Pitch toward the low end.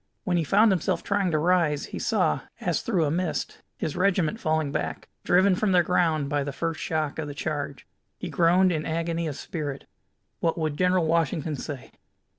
No: medium, 165 Hz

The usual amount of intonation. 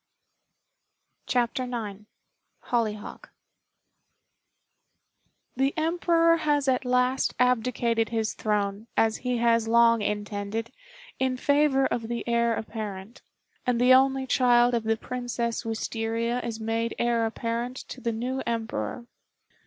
No: narrow, 2.0 semitones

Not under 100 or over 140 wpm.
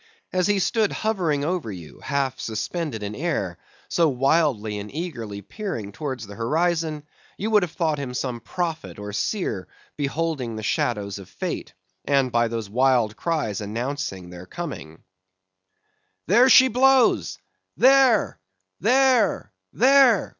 Yes: slow, 135 wpm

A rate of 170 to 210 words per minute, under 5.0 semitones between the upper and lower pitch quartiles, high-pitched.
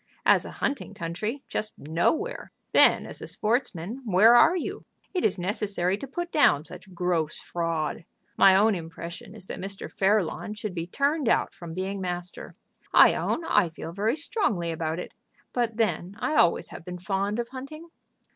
No: average, 175 wpm; wide, 5.4 semitones; high, 195 Hz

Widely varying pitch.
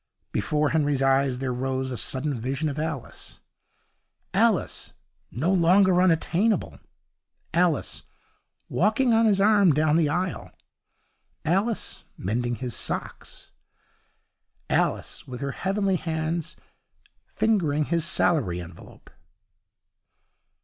Yes: wide, 5.7 semitones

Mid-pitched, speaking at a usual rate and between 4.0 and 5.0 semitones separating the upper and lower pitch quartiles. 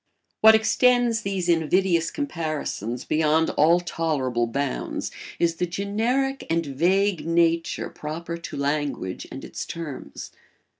No: medium, 165 Hz; slow, 115 wpm; average, 4.5 semitones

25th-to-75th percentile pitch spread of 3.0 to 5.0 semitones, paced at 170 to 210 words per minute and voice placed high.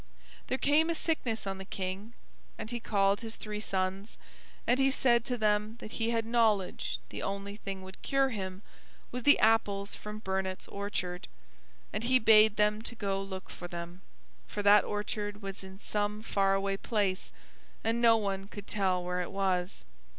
No: narrow, 2.6 semitones; average, 180 wpm; high, 205 Hz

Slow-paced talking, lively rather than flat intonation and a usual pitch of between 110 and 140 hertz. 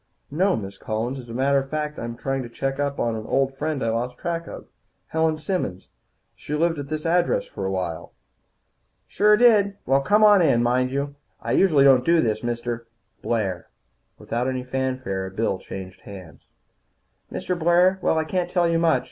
No: average, 195 wpm; wide, 5.9 semitones; low, 135 Hz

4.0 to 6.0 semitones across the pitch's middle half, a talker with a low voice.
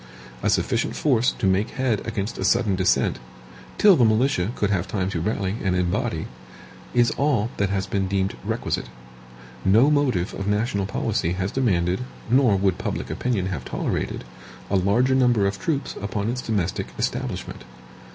Yes: average, 4.3 semitones; low, 100 Hz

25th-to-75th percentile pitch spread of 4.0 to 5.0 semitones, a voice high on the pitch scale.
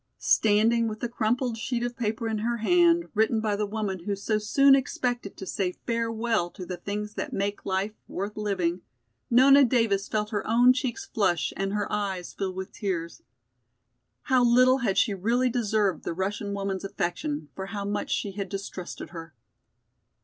No: average, 3.3 semitones; high, 210 Hz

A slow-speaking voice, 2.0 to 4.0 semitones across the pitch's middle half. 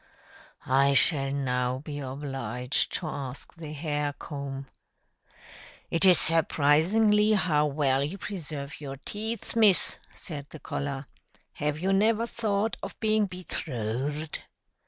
No: slow, 120 wpm; average, 4.9 semitones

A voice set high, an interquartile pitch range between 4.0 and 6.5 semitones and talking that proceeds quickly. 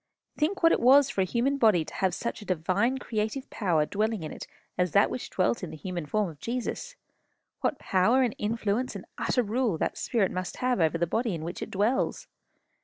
Yes: high, 210 Hz; wide, 5.4 semitones; fast, 215 wpm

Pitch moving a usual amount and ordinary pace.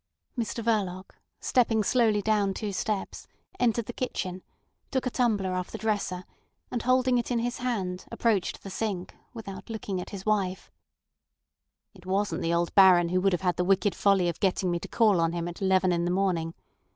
Yes: average, 3.5 semitones; average, 190 wpm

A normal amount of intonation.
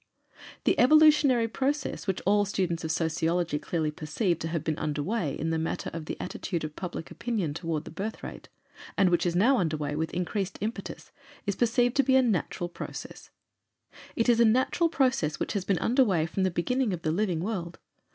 No: wide, 6.2 semitones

